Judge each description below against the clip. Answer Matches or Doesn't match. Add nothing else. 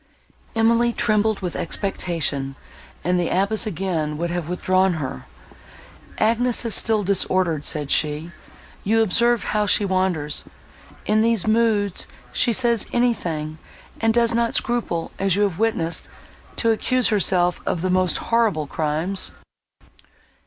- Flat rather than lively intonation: Doesn't match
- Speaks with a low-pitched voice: Doesn't match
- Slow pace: Matches